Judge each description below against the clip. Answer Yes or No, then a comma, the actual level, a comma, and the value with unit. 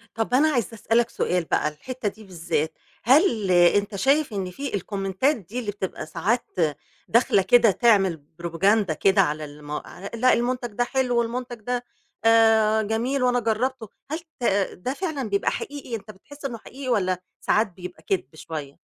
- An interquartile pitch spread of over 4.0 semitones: Yes, average, 4.8 semitones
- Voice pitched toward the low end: No, high, 220 Hz